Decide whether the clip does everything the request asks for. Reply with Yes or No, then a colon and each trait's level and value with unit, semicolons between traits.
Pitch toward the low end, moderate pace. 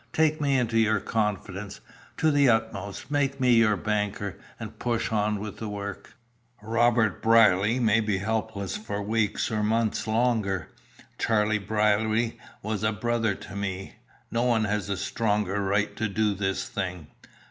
Yes: low, 110 Hz; average, 150 wpm